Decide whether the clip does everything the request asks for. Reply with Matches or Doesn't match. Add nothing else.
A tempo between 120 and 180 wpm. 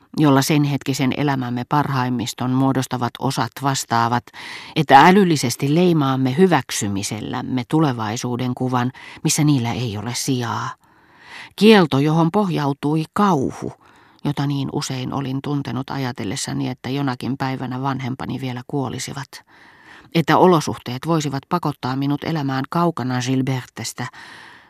Doesn't match